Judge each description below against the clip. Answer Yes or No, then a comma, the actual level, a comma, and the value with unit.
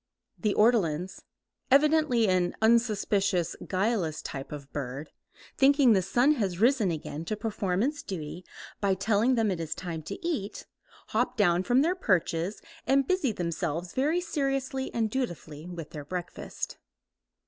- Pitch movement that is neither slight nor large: No, wide, 6.8 semitones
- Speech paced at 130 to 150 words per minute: Yes, average, 145 wpm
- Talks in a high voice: Yes, high, 205 Hz